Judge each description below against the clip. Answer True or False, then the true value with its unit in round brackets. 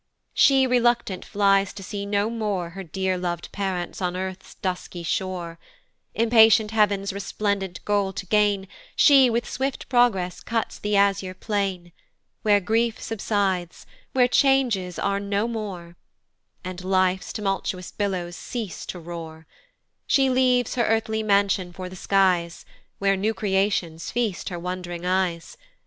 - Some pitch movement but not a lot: True (3.2 semitones)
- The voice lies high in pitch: True (195 Hz)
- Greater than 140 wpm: False (135 wpm)